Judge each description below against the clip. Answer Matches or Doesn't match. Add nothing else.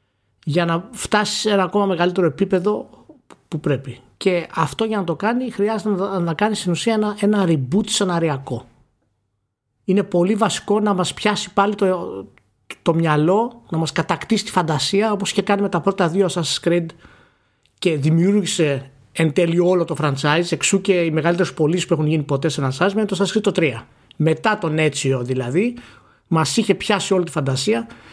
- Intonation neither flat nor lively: Matches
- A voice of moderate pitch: Matches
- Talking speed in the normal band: Doesn't match